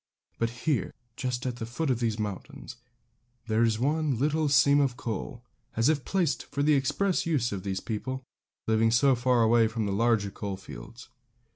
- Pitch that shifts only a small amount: No, average, 4.0 semitones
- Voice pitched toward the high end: No, low, 120 Hz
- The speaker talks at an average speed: Yes, average, 180 wpm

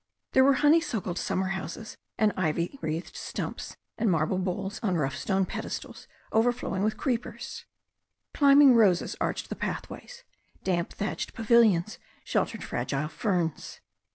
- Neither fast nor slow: No, slow, 125 wpm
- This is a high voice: Yes, high, 200 Hz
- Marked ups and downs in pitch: No, average, 5.0 semitones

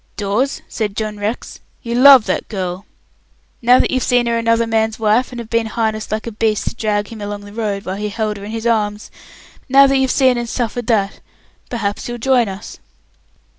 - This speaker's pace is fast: Yes, fast, 210 wpm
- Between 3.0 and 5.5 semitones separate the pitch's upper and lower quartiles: No, narrow, 2.5 semitones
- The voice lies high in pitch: Yes, high, 225 Hz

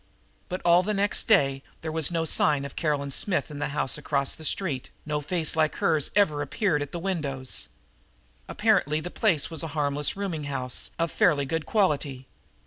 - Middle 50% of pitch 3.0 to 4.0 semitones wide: Yes, average, 3.3 semitones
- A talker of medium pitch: Yes, medium, 150 Hz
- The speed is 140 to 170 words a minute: No, average, 190 wpm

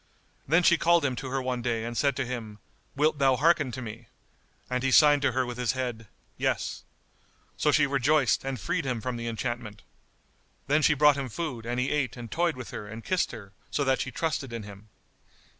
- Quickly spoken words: Yes, fast, 215 wpm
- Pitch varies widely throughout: No, average, 3.4 semitones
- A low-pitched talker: Yes, low, 130 Hz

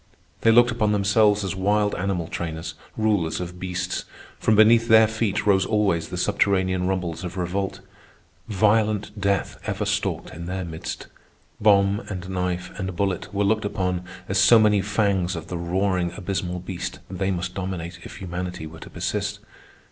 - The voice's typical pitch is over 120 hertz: No, very low, 95 Hz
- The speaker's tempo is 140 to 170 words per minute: Yes, average, 165 wpm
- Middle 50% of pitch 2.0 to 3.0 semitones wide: Yes, narrow, 2.5 semitones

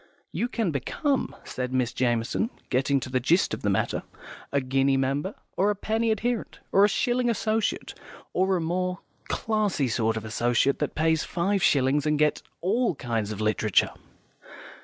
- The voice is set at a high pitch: No, medium, 150 Hz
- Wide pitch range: Yes, wide, 8.1 semitones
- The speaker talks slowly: No, average, 165 wpm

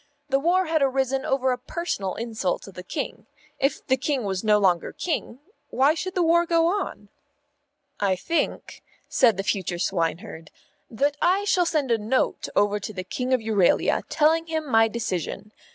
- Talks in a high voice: Yes, very high, 255 Hz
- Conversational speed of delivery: Yes, average, 175 wpm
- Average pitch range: No, wide, 7.6 semitones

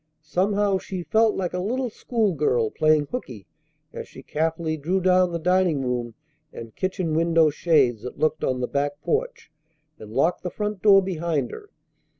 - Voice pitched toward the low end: No, medium, 170 Hz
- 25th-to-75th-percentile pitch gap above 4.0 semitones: Yes, average, 4.9 semitones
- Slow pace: No, average, 165 wpm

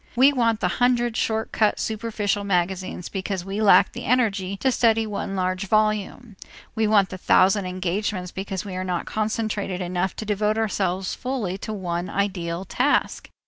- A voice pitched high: Yes, high, 200 Hz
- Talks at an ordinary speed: Yes, average, 165 wpm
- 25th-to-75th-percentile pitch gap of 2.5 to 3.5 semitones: Yes, average, 2.9 semitones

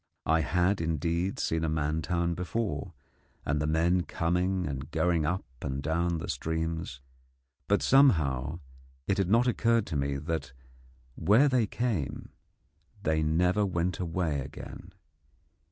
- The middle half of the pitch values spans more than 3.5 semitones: No, average, 3.0 semitones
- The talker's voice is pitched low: Yes, very low, 85 Hz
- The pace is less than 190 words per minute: Yes, slow, 135 wpm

